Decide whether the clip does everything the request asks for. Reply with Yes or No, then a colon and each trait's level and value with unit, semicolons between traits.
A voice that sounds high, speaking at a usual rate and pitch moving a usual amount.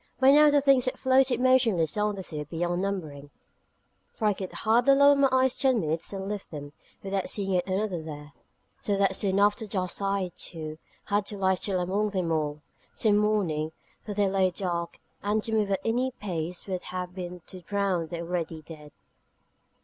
Yes: high, 195 Hz; average, 195 wpm; average, 3.7 semitones